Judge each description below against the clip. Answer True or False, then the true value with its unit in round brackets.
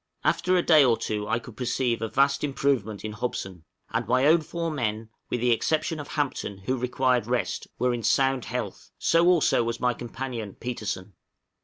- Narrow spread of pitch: False (3.9 semitones)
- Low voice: True (125 Hz)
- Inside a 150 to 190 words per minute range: True (185 wpm)